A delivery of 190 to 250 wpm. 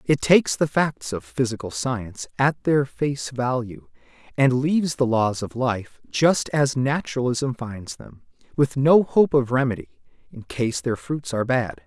No: average, 165 wpm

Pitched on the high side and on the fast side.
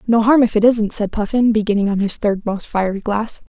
Yes: high, 215 Hz; fast, 235 wpm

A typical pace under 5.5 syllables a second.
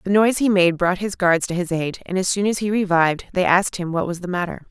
No: 6.3 syllables/s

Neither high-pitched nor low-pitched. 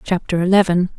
Yes: medium, 180 Hz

